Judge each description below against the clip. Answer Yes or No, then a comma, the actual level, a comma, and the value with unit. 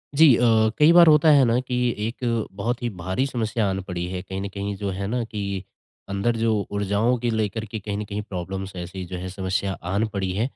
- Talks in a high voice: No, low, 100 Hz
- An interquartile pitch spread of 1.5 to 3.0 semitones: No, average, 3.5 semitones